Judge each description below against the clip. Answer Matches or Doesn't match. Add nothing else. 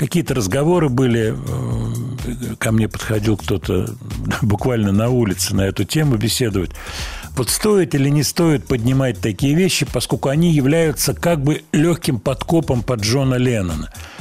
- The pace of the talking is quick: Doesn't match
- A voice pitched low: Matches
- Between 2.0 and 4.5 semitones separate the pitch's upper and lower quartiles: Doesn't match